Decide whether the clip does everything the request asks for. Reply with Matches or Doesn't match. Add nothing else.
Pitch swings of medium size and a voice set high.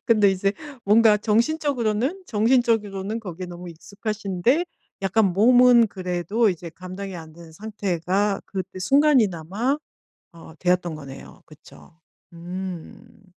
Matches